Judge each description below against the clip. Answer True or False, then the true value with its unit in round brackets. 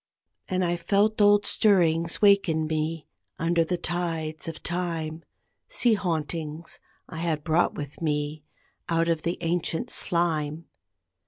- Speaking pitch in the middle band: True (165 Hz)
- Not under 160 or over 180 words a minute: False (135 wpm)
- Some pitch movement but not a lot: False (2.0 semitones)